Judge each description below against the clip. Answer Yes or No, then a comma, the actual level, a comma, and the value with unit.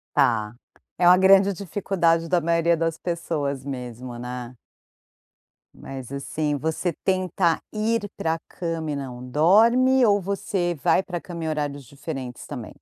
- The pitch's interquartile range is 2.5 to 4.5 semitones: No, average, 5.0 semitones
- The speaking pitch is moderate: Yes, medium, 165 Hz